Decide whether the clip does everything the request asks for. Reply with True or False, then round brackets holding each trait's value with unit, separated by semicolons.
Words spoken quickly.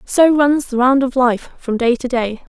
True (235 wpm)